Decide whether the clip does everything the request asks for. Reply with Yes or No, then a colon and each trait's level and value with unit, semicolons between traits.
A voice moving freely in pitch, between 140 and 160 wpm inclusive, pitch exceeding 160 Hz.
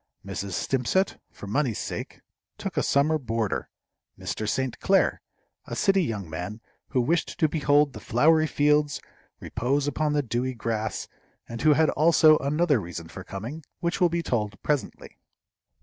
No: wide, 5.8 semitones; average, 155 wpm; medium, 140 Hz